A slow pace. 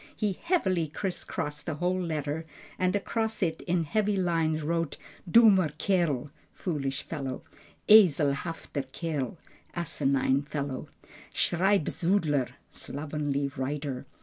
Yes: slow, 105 wpm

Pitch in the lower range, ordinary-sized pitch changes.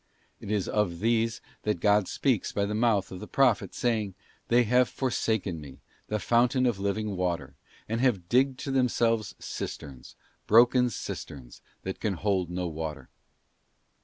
Yes: low, 105 Hz; average, 4.6 semitones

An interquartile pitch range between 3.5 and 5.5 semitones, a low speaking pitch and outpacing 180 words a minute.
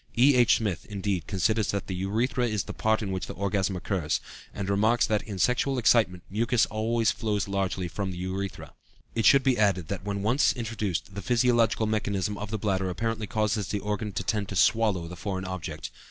No: average, 2.9 semitones; low, 105 Hz; average, 195 wpm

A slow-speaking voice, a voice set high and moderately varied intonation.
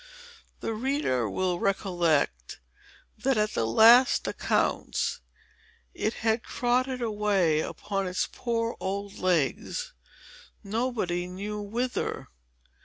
Yes: slow, 100 wpm; high, 210 Hz; average, 4.6 semitones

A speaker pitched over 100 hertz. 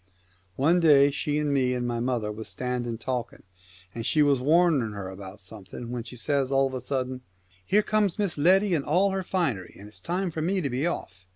Yes: low, 135 Hz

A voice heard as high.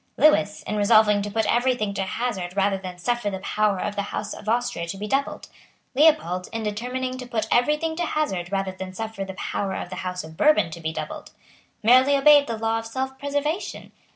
Yes: high, 215 Hz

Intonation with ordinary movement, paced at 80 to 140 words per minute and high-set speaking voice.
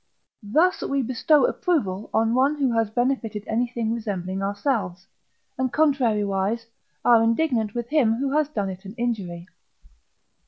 Yes: average, 4.6 semitones; slow, 135 wpm; high, 230 Hz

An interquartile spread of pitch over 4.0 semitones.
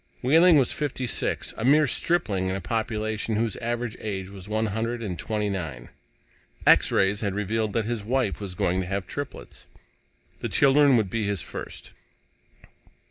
No: average, 3.6 semitones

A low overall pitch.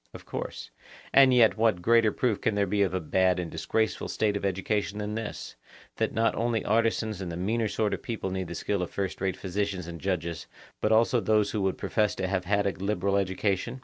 Yes: low, 100 Hz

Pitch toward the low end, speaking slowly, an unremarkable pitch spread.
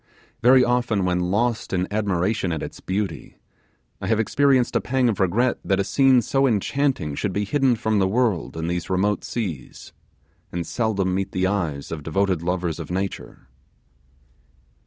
No: low, 100 Hz; average, 165 wpm; average, 4.9 semitones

